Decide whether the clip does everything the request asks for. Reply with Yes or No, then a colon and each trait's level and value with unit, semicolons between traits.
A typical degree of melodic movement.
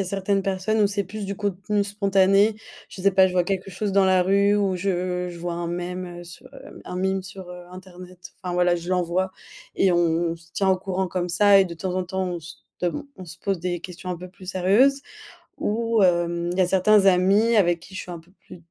No: narrow, 1.8 semitones